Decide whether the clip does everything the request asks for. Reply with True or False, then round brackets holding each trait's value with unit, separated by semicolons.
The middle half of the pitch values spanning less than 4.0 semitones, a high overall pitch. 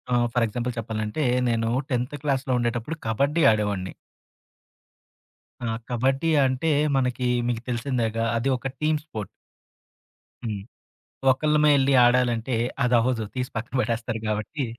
False (2.9 semitones; 120 Hz)